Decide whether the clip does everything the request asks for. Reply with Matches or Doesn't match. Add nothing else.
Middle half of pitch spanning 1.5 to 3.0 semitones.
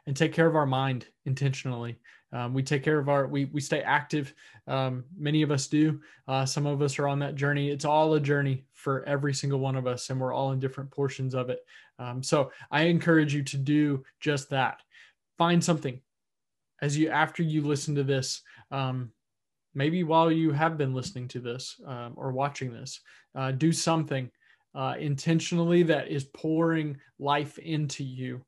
Matches